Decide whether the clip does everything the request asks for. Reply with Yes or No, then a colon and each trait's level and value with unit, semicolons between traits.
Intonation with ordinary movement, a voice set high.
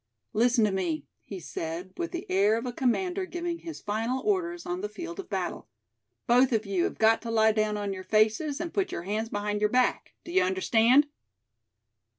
No: wide, 8.5 semitones; high, 230 Hz